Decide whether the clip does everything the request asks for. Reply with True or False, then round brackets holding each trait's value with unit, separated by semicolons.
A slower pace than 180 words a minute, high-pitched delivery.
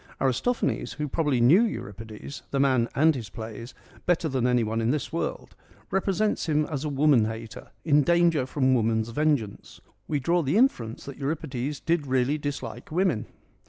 False (170 wpm; 140 Hz)